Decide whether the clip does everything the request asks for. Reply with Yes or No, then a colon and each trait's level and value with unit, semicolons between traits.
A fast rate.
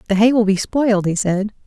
Yes: fast, 250 wpm